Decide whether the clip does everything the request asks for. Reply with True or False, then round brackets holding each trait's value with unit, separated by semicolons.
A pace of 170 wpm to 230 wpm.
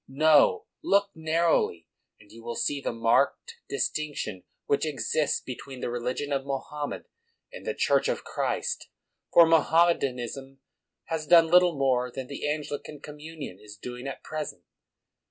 False (155 wpm)